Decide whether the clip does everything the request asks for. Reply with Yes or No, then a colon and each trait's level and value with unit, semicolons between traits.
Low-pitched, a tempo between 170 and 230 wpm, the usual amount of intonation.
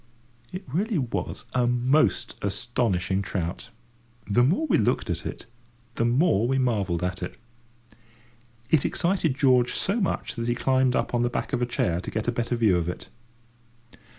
Yes: low, 120 Hz; average, 175 wpm; average, 4.7 semitones